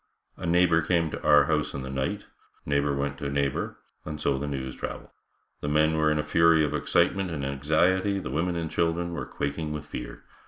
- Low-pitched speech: Yes, very low, 75 Hz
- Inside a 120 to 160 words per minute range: No, fast, 205 wpm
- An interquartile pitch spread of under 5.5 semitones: Yes, average, 2.9 semitones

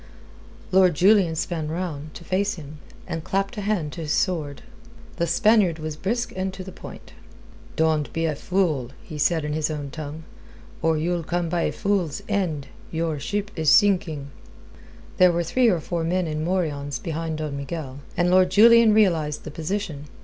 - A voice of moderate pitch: Yes, medium, 165 Hz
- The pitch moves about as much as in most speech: Yes, average, 3.5 semitones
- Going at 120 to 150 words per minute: No, average, 180 wpm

